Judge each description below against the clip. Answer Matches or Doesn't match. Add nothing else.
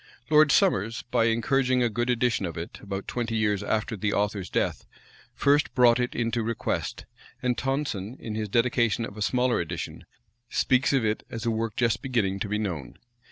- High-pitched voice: Doesn't match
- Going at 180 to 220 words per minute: Matches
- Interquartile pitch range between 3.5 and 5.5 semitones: Doesn't match